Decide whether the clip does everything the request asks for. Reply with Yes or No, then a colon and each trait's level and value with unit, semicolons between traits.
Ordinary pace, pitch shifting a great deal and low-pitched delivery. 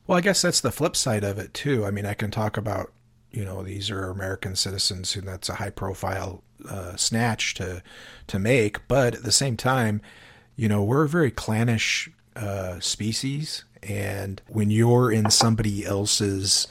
No: average, 185 wpm; average, 3.1 semitones; low, 105 Hz